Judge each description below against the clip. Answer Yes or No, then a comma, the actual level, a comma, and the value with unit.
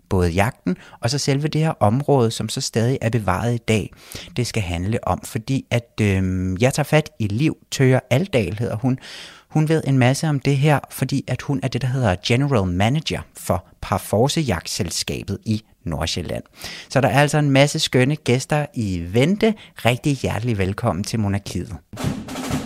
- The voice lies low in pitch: Yes, low, 120 Hz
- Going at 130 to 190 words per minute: Yes, average, 170 wpm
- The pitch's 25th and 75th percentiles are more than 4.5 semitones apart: Yes, average, 5.0 semitones